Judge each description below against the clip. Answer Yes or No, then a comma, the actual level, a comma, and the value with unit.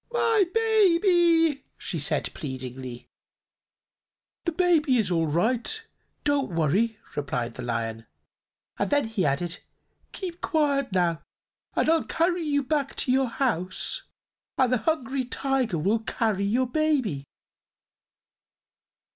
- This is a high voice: Yes, very high, 255 Hz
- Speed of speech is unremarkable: No, slow, 120 wpm